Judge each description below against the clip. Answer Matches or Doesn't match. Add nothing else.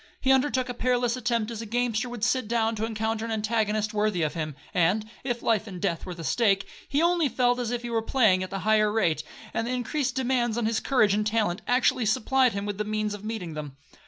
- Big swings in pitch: Doesn't match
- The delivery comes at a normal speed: Doesn't match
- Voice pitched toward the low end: Doesn't match